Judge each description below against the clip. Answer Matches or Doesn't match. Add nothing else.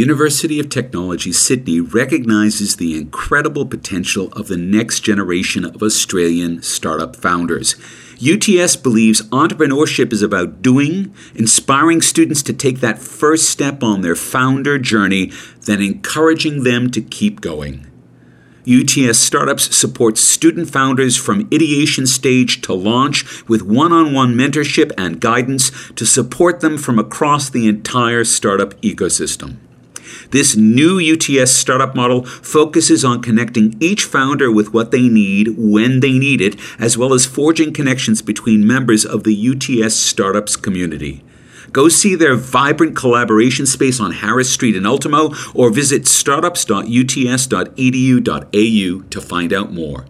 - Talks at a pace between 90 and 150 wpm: Matches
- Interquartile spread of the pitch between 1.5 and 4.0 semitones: Doesn't match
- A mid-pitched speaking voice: Doesn't match